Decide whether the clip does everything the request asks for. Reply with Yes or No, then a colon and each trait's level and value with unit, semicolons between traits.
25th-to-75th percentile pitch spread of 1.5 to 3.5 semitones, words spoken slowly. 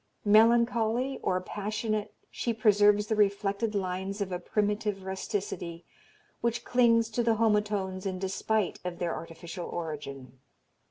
Yes: average, 3.0 semitones; slow, 125 wpm